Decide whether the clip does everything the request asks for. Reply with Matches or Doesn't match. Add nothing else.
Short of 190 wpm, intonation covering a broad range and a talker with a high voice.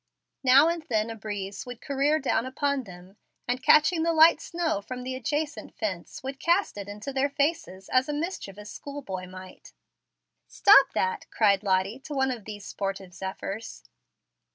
Matches